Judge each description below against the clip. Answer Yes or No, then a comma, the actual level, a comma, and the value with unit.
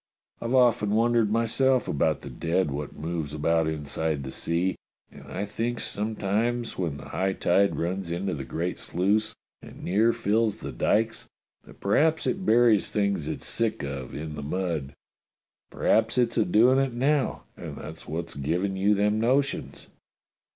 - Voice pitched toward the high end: No, low, 100 Hz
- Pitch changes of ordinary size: No, wide, 5.8 semitones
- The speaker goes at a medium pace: Yes, average, 165 wpm